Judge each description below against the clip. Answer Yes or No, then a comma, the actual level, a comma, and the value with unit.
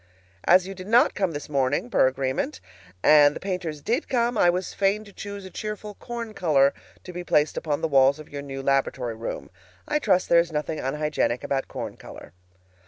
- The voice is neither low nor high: Yes, medium, 165 Hz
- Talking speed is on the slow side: No, average, 200 wpm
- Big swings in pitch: Yes, wide, 6.1 semitones